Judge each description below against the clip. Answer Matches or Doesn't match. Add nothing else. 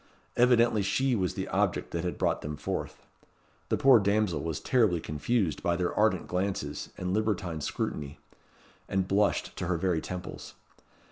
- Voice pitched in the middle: Doesn't match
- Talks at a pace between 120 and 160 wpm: Matches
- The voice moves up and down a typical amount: Matches